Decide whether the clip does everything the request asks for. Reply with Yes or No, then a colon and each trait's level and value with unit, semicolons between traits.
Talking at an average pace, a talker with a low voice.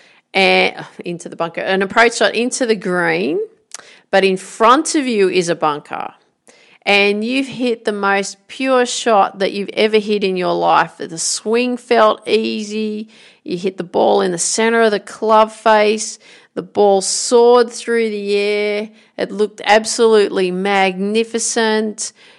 No: average, 155 wpm; high, 210 Hz